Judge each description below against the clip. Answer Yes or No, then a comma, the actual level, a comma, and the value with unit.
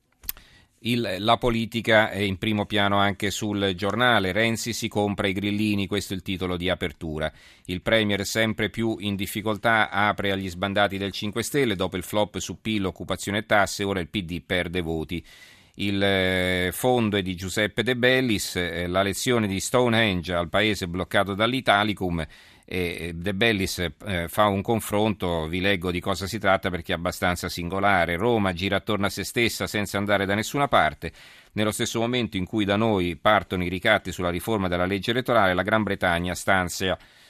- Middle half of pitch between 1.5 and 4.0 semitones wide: Yes, average, 2.9 semitones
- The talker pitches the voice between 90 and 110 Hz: Yes, low, 100 Hz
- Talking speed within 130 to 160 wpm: No, fast, 170 wpm